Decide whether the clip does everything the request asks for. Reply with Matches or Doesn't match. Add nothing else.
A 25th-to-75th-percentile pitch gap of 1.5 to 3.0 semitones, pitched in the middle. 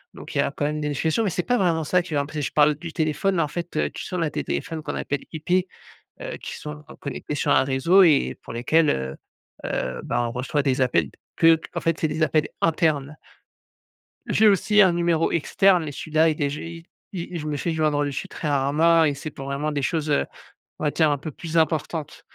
Matches